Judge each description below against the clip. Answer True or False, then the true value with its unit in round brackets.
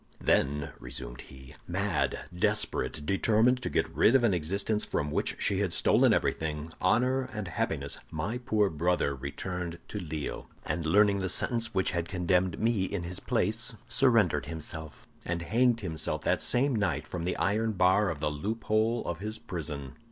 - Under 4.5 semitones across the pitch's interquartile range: False (5.3 semitones)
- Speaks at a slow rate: False (165 wpm)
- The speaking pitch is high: False (90 Hz)